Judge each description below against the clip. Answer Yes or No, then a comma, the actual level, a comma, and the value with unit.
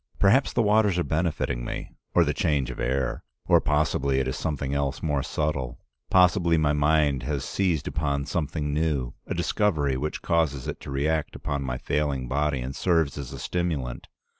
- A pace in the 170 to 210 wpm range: Yes, average, 180 wpm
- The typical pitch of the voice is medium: No, very low, 75 Hz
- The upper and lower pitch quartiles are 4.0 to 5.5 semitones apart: No, average, 3.1 semitones